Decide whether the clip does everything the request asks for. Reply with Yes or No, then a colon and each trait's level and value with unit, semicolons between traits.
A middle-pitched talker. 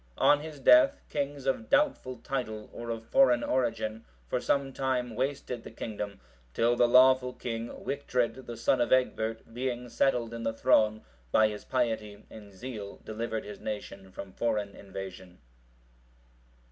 No: low, 115 Hz